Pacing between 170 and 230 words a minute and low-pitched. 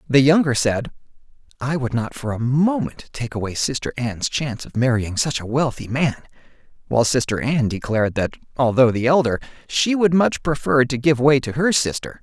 Yes: average, 185 wpm; low, 130 Hz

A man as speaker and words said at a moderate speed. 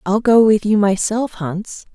No: female; average, 185 wpm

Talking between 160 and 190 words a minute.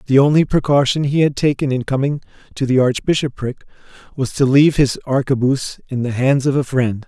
Yes: average, 185 wpm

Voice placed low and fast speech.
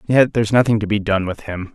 Yes: low, 105 Hz; fast, 275 wpm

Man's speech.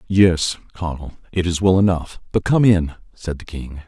Yes: male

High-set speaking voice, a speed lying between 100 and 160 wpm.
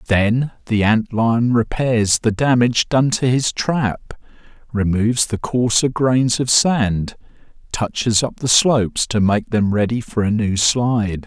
No: low, 115 Hz; average, 155 wpm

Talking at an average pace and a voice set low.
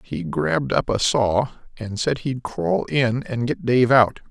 Yes: average, 195 wpm; low, 120 Hz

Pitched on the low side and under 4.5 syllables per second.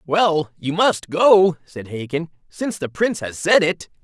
No: medium, 165 Hz; 4.3 syllables/s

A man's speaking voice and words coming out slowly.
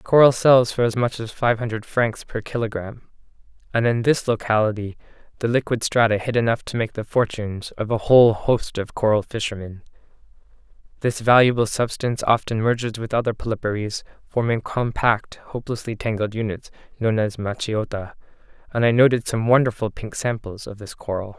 No: male; average, 160 wpm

